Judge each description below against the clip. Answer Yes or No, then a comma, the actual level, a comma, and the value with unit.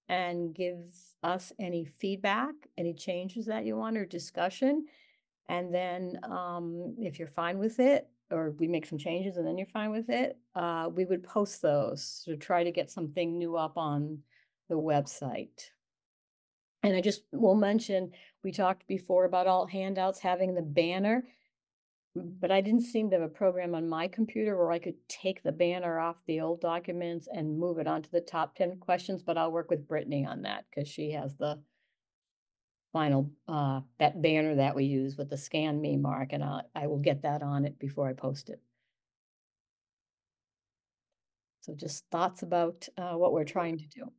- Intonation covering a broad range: No, average, 3.7 semitones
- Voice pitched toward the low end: No, medium, 170 Hz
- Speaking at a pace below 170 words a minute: No, average, 180 wpm